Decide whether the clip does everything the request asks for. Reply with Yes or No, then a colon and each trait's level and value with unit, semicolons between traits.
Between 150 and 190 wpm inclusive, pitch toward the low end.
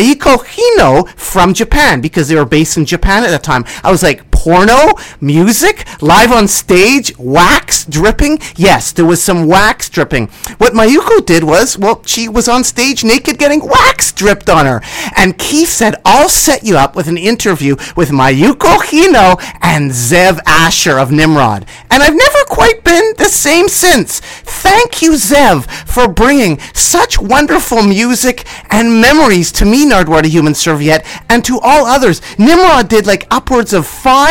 No: average, 165 wpm; high, 220 Hz